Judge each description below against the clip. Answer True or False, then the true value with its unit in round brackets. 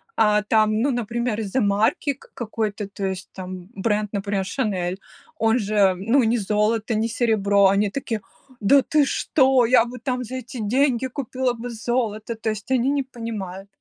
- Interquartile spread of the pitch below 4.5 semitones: True (3.5 semitones)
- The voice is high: True (225 Hz)